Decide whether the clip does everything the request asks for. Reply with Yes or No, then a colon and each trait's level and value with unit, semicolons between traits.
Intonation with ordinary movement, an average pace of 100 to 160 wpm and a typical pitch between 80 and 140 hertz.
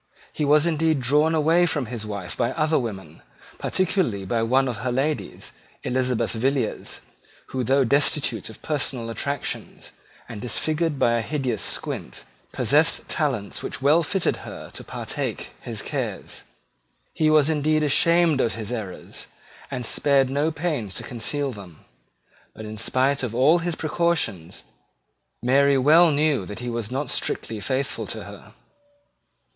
Yes: average, 4.8 semitones; average, 150 wpm; low, 135 Hz